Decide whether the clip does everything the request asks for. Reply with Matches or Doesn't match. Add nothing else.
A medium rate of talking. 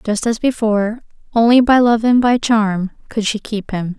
Matches